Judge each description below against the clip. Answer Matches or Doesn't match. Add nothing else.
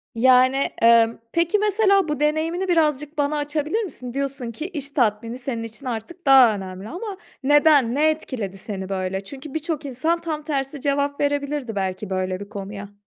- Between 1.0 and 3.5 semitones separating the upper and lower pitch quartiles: Doesn't match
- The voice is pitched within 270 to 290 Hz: Matches